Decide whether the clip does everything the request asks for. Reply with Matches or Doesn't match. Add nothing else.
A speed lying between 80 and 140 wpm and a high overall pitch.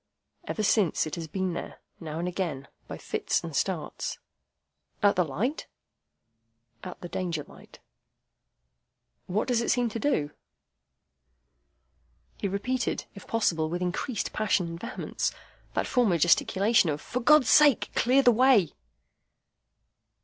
Matches